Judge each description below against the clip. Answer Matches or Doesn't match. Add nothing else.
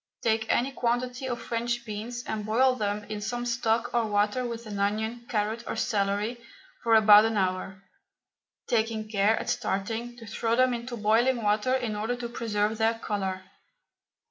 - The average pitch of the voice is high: Matches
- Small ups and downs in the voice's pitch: Matches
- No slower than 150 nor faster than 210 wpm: Matches